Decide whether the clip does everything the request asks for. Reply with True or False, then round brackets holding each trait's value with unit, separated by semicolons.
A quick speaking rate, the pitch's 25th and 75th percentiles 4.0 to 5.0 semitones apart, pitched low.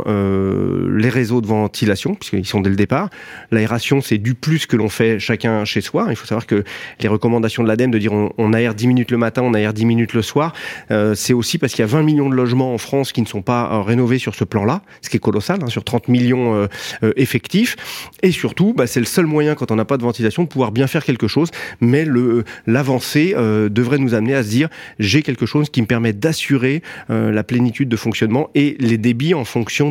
False (245 wpm; 3.5 semitones; 120 Hz)